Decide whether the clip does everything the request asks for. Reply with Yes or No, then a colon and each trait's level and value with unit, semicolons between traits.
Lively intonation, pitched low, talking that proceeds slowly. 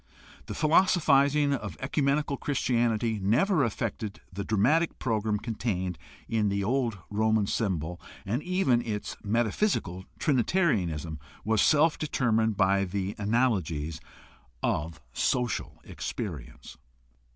Yes: wide, 5.7 semitones; low, 110 Hz; slow, 105 wpm